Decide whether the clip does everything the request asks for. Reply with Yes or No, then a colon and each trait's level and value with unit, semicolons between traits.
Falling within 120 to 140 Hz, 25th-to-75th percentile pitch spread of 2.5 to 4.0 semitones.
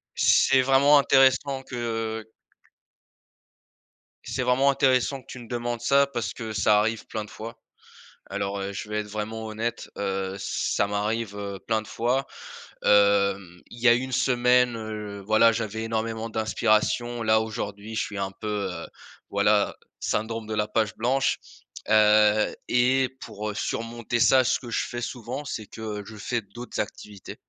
No: low, 110 Hz; average, 2.8 semitones